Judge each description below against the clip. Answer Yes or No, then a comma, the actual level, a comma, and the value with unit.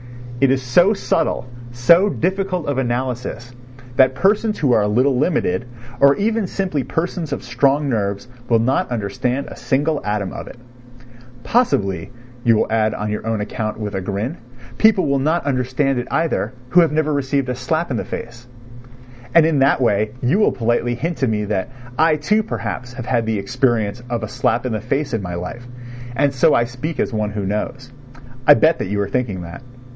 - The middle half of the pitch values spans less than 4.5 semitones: No, average, 5.3 semitones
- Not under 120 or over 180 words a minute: No, average, 195 wpm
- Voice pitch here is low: Yes, low, 125 Hz